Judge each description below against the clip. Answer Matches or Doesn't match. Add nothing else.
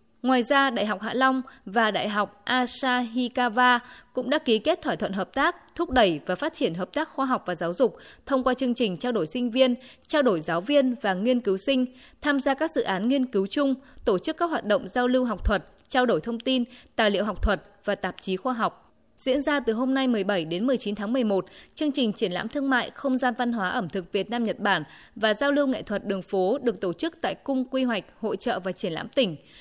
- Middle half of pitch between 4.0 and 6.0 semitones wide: Matches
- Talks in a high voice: Matches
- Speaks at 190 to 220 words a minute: Doesn't match